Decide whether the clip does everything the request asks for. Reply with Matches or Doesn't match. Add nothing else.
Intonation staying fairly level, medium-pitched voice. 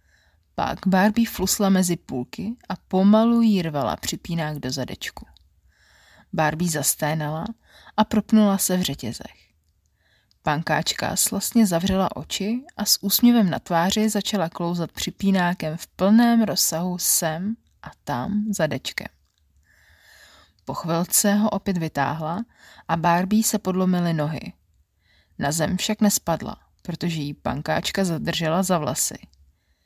Doesn't match